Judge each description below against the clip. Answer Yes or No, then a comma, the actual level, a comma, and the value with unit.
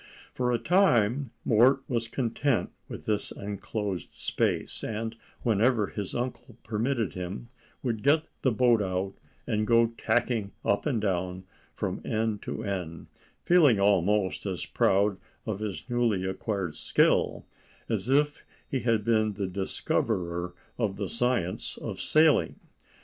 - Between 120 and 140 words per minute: Yes, slow, 135 wpm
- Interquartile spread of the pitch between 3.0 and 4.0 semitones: Yes, average, 3.6 semitones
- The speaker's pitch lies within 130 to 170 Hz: No, low, 110 Hz